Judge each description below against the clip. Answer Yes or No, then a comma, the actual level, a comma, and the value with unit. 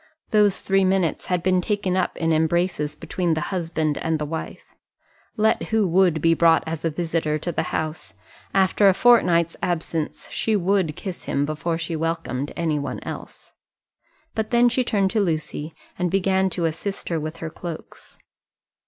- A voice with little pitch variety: No, average, 3.2 semitones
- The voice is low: No, medium, 170 Hz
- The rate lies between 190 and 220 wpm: No, average, 170 wpm